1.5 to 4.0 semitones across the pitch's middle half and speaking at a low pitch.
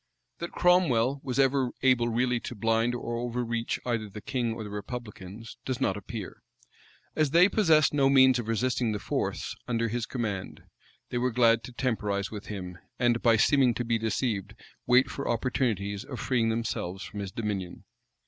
Yes: average, 3.0 semitones; low, 115 Hz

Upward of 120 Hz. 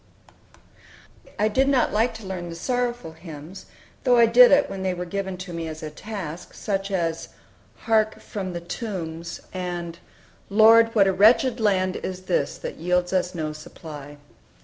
Yes: medium, 185 Hz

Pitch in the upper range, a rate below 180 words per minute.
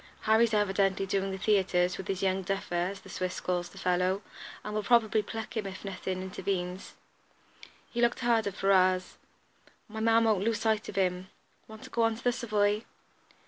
No: high, 195 Hz; average, 185 wpm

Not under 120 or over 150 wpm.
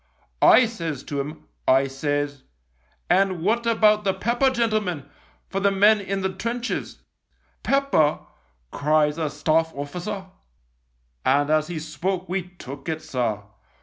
No: average, 160 wpm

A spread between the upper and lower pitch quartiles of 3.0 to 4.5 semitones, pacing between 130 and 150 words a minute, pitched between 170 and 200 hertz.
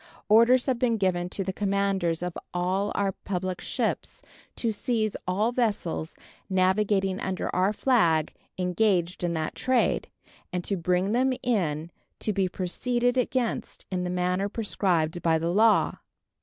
Yes: average, 3.6 semitones; average, 145 wpm; high, 190 Hz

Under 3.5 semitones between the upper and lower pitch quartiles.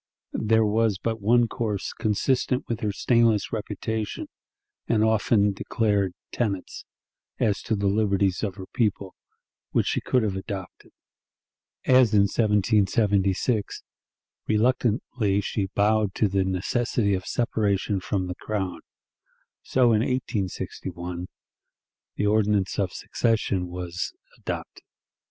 Yes: narrow, 2.6 semitones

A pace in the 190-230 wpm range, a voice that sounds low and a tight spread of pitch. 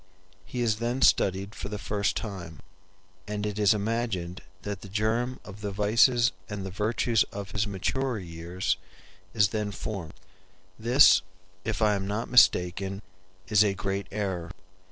No: average, 155 wpm; low, 105 Hz; narrow, 2.3 semitones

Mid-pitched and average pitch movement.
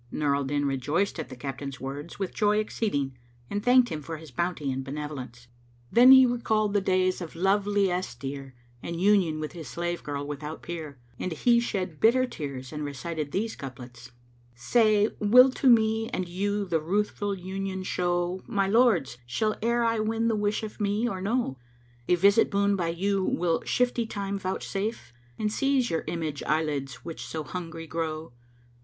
No: medium, 180 Hz; wide, 5.9 semitones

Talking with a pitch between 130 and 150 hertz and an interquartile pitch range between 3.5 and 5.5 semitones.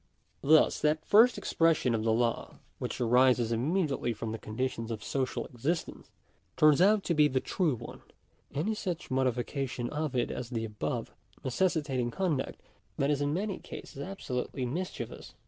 Yes: low, 135 Hz; average, 5.2 semitones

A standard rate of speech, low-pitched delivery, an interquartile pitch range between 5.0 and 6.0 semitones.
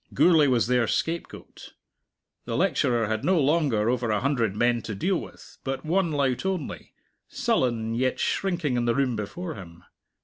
Yes: average, 165 wpm; low, 125 Hz; wide, 5.5 semitones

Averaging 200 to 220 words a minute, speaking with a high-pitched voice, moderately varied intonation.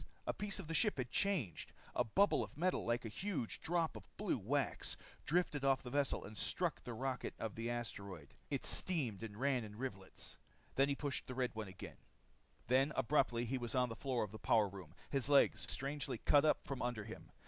No: fast, 205 wpm; low, 130 Hz; average, 4.4 semitones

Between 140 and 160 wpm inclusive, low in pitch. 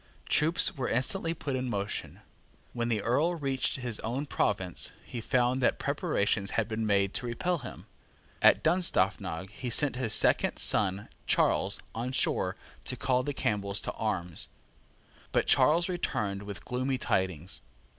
Yes: average, 150 wpm; low, 120 Hz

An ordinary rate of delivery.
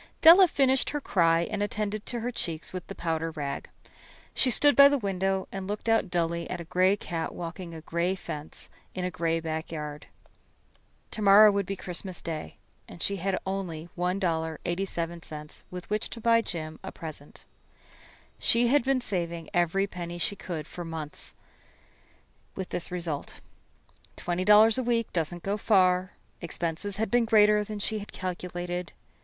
Yes: average, 160 wpm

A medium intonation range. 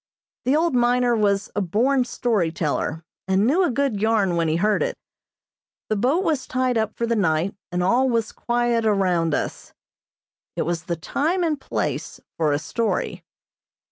No: wide, 5.8 semitones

